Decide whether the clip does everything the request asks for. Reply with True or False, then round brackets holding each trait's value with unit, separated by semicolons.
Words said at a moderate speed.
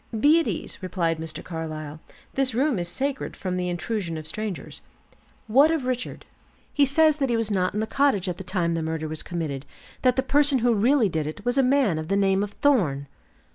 False (215 wpm)